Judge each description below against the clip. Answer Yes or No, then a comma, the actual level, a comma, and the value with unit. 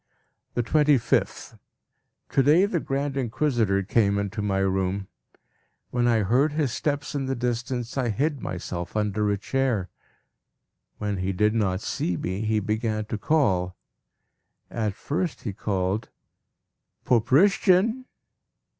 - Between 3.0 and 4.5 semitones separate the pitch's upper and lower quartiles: No, wide, 5.4 semitones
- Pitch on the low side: Yes, low, 115 Hz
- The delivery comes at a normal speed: No, slow, 130 wpm